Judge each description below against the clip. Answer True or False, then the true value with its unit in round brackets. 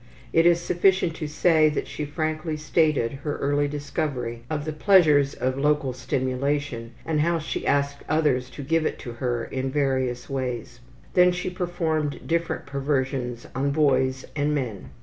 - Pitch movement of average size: True (3.1 semitones)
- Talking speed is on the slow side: False (160 wpm)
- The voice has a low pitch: False (145 Hz)